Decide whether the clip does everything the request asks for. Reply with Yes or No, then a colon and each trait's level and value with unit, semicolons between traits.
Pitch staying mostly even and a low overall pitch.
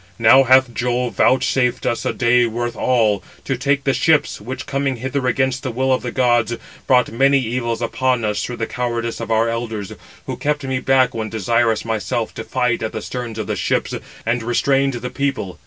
Yes: narrow, 2.2 semitones; low, 120 Hz